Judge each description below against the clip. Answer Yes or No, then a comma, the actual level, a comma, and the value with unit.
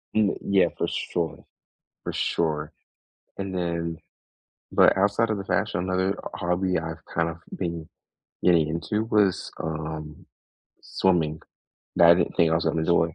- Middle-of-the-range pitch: No, very low, 85 Hz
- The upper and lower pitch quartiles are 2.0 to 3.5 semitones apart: Yes, average, 2.7 semitones